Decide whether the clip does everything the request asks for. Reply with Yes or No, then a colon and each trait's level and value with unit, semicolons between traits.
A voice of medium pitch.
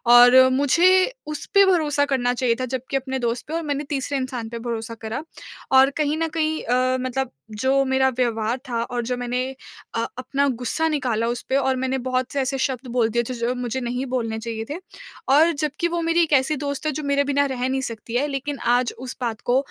No: very high, 260 Hz